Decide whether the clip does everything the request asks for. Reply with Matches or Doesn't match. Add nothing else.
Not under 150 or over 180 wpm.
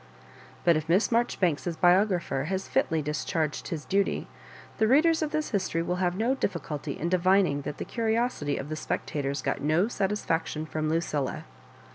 Matches